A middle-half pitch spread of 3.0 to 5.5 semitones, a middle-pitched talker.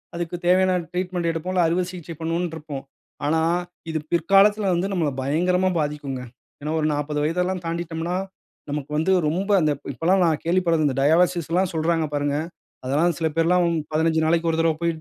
No: narrow, 2.5 semitones; medium, 165 Hz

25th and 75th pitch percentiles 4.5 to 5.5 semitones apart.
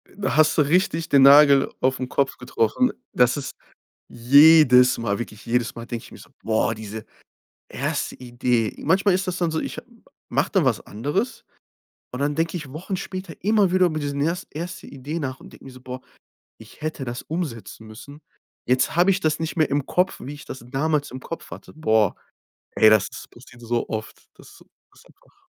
Yes: average, 5.2 semitones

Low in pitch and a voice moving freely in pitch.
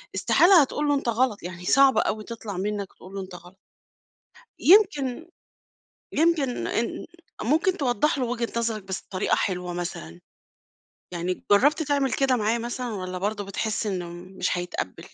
No: high, 220 Hz; wide, 6.5 semitones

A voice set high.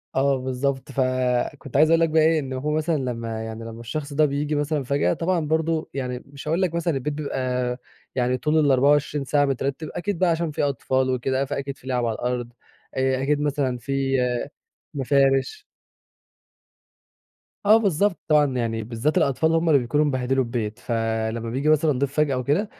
No: medium, 140 Hz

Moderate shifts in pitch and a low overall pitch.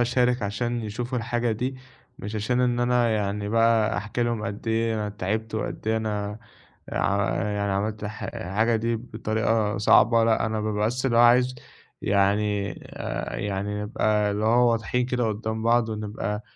No: narrow, 2.2 semitones; low, 110 Hz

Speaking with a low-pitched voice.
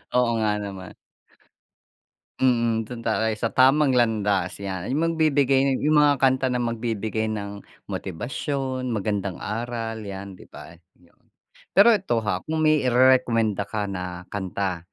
Yes: low, 115 Hz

